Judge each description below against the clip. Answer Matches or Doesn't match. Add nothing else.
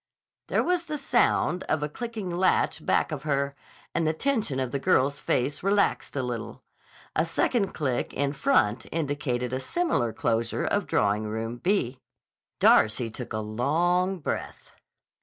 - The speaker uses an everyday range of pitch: Doesn't match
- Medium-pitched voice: Matches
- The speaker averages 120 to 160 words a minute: Matches